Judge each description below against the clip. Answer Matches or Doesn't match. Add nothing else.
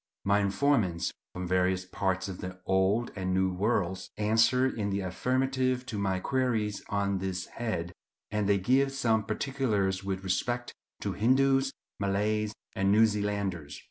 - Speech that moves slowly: Doesn't match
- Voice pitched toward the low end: Matches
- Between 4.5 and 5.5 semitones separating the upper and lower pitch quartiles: Doesn't match